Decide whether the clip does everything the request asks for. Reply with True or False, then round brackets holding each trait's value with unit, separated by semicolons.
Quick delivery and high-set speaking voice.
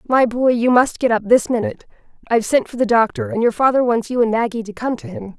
True (265 wpm; 235 Hz)